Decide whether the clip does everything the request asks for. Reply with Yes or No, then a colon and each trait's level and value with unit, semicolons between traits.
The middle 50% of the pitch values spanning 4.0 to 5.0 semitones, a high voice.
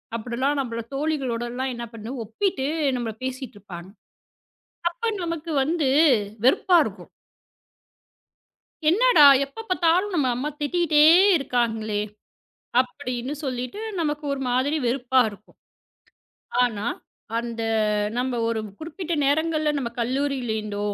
Yes: average, 4.7 semitones; very high, 265 Hz